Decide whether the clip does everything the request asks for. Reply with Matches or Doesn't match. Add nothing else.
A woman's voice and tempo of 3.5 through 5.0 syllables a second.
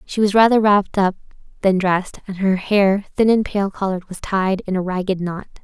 Doesn't match